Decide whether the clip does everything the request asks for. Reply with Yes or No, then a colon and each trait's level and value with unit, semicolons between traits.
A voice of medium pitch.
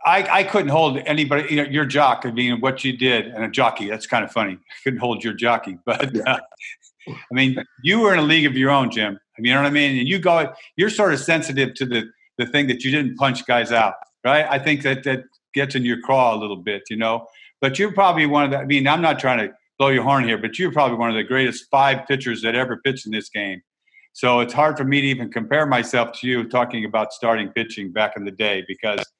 No: low, 130 Hz